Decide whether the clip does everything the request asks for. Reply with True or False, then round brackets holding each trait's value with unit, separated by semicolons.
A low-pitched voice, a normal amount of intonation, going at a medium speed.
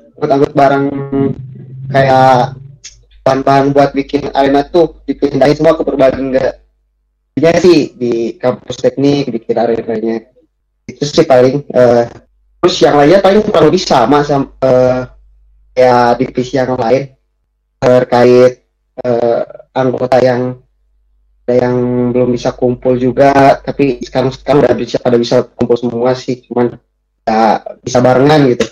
False (125 Hz; 2.3 semitones; 120 wpm)